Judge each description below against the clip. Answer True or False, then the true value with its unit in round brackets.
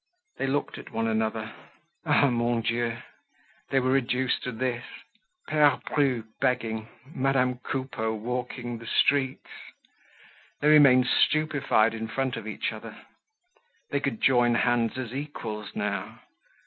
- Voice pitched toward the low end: True (125 Hz)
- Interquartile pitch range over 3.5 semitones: False (2.9 semitones)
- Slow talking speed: True (125 wpm)